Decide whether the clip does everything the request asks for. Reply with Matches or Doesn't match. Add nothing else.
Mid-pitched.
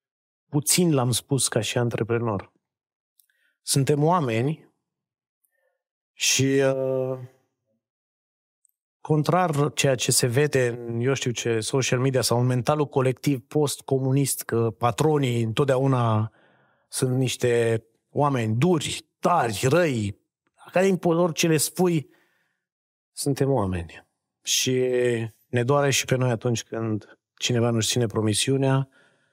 Doesn't match